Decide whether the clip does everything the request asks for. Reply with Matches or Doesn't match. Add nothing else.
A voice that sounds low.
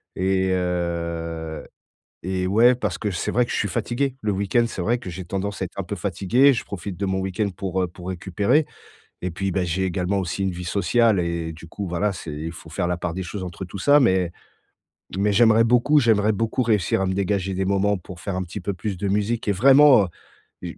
Matches